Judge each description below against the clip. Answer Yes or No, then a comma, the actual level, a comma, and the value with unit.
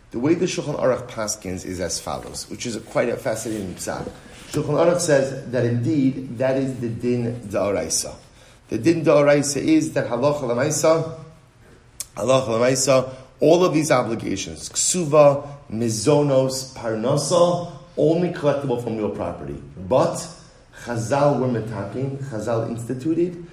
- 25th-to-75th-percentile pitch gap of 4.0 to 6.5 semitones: Yes, average, 4.3 semitones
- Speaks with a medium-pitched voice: No, low, 130 Hz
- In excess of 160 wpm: No, slow, 135 wpm